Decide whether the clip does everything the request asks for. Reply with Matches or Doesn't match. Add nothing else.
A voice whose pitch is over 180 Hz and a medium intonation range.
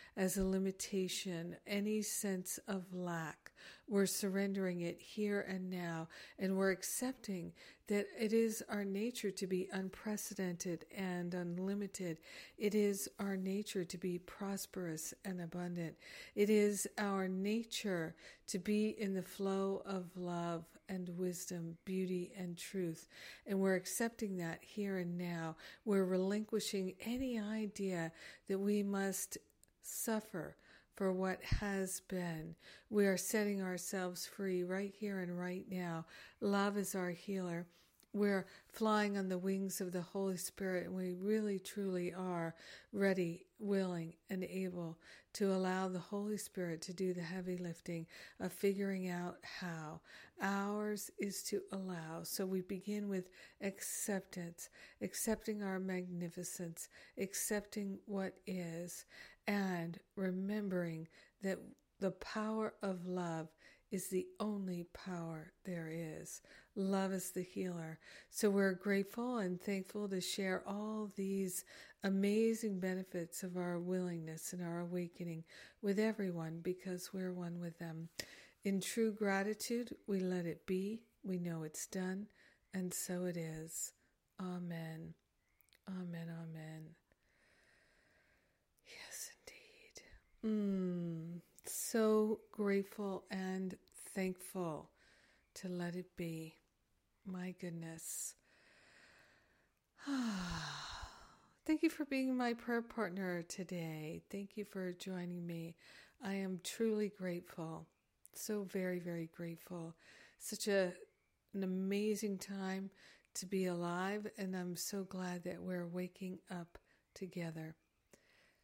Doesn't match